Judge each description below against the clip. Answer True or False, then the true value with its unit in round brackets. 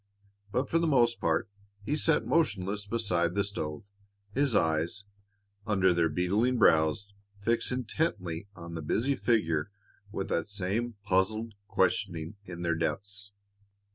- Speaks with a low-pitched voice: True (100 Hz)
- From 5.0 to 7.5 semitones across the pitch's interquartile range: True (5.3 semitones)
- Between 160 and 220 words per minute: False (135 wpm)